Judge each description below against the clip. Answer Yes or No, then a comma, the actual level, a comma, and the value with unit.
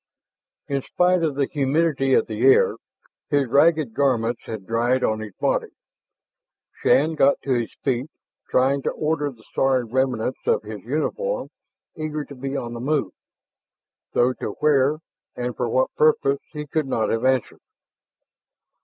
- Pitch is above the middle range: No, low, 135 Hz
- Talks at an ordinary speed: Yes, average, 155 wpm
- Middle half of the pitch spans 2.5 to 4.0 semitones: Yes, average, 3.6 semitones